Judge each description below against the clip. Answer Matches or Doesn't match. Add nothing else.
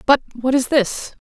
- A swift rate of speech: Doesn't match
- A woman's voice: Matches